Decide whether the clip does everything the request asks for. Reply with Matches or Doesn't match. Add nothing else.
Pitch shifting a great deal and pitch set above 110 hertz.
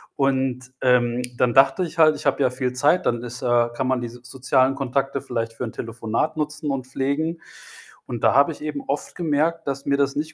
Doesn't match